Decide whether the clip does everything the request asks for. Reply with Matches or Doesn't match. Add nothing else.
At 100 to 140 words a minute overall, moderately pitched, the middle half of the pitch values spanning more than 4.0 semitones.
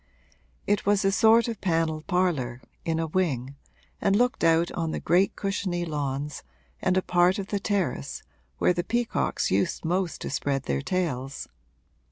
Doesn't match